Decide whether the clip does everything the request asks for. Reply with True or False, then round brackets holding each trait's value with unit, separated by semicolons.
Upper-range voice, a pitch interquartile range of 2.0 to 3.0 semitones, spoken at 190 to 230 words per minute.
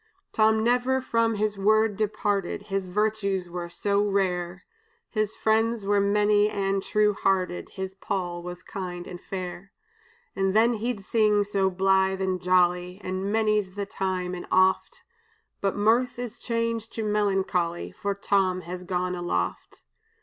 False (195 Hz; 2.6 semitones; 145 wpm)